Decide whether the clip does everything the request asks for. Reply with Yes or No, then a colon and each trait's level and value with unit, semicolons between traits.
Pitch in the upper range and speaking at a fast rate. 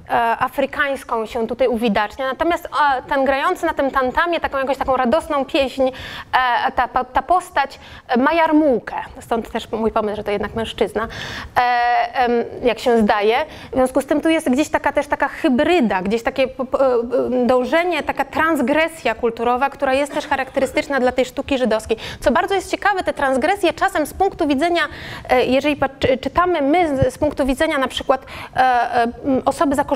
No: very high, 275 Hz; average, 150 wpm